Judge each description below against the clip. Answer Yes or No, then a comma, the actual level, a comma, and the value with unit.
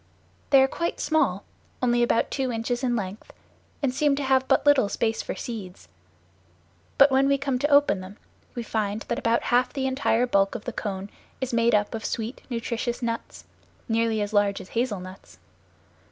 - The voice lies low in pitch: No, high, 235 Hz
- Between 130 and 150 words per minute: No, average, 185 wpm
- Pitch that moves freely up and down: No, average, 4.0 semitones